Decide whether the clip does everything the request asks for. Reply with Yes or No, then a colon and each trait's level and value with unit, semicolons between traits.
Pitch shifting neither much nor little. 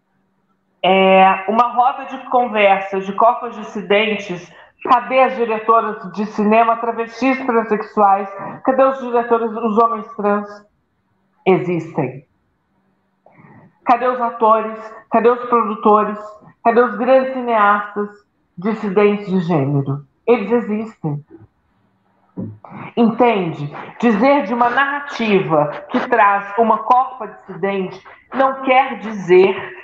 Yes: average, 3.9 semitones